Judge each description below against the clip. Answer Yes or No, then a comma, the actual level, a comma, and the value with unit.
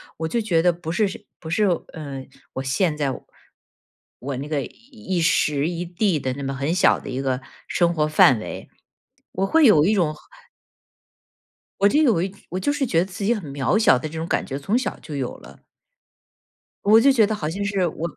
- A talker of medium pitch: Yes, medium, 170 Hz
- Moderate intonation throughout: No, wide, 5.8 semitones